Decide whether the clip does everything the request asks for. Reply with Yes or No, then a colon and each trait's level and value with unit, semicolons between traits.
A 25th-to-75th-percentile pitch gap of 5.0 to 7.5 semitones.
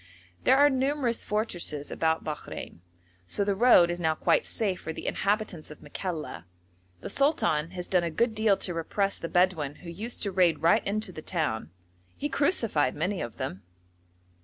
Yes: wide, 5.4 semitones